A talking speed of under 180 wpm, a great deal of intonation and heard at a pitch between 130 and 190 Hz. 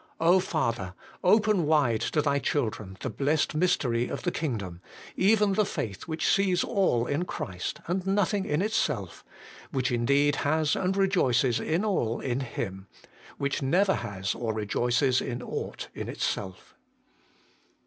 Yes: average, 145 wpm; wide, 7.8 semitones; medium, 140 Hz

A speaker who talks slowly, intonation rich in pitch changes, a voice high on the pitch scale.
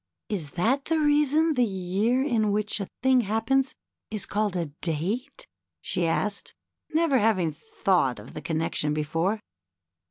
No: average, 150 wpm; wide, 7.1 semitones; high, 210 Hz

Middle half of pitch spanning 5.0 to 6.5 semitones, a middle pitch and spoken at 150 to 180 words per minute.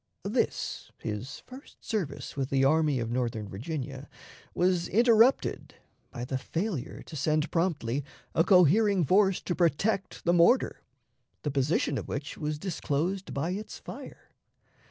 No: wide, 5.6 semitones; medium, 160 Hz; slow, 135 wpm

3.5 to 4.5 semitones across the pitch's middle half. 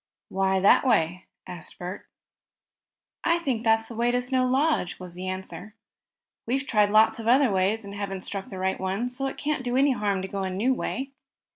No: average, 5.1 semitones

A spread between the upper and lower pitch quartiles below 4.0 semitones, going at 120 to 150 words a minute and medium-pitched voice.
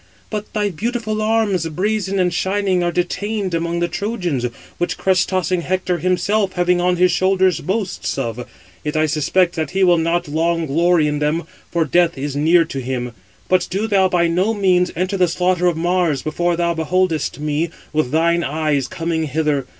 No: average, 2.9 semitones; average, 180 wpm; medium, 175 Hz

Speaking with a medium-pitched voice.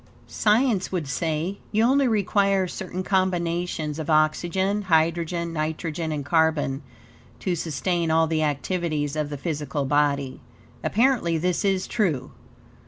Yes: medium, 165 Hz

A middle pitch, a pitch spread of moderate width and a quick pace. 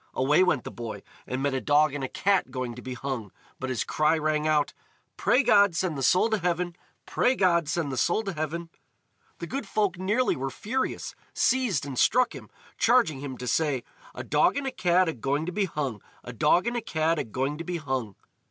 No: medium, 155 Hz; wide, 5.8 semitones; fast, 215 wpm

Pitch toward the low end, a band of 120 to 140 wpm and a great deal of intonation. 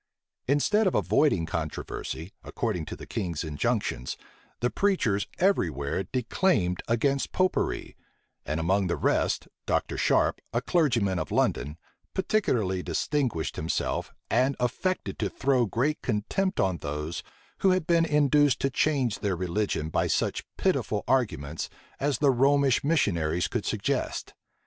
Yes: low, 120 Hz; slow, 135 wpm; wide, 9.0 semitones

